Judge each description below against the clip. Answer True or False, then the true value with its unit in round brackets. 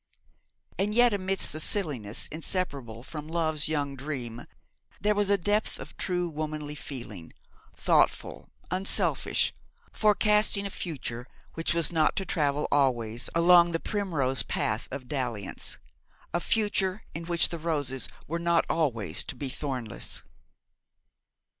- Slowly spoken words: True (130 wpm)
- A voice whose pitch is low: False (155 Hz)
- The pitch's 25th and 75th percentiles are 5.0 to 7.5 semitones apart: True (5.6 semitones)